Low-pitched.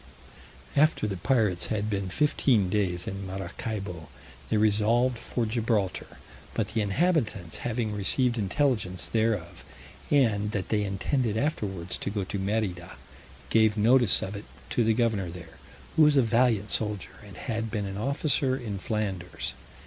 Yes: low, 105 Hz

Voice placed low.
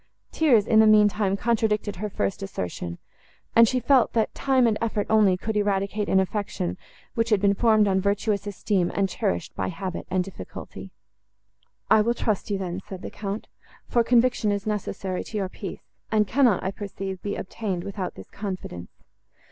No: high, 205 Hz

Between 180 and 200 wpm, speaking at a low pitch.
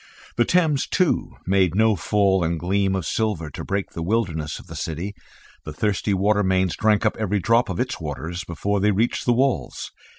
Yes: average, 195 wpm; low, 100 Hz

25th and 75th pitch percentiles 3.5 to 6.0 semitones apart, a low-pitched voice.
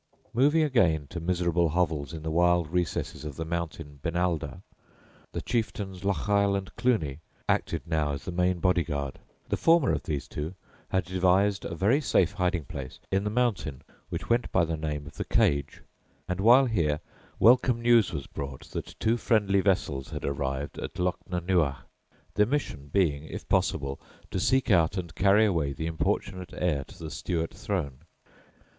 Yes: average, 4.6 semitones; very low, 90 Hz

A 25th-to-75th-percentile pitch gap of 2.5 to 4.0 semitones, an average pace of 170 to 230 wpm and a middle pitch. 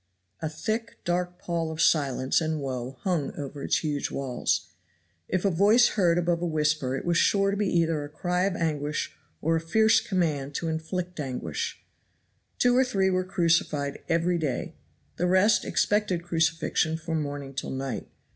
Yes: average, 3.6 semitones; average, 175 wpm; medium, 165 Hz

